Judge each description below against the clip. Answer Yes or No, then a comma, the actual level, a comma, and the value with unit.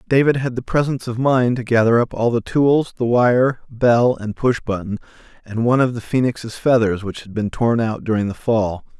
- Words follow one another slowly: No, fast, 205 wpm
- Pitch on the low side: Yes, low, 120 Hz